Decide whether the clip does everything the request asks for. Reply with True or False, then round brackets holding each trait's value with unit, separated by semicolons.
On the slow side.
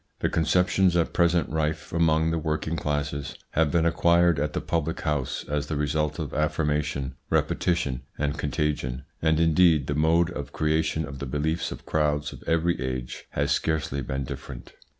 False (170 wpm)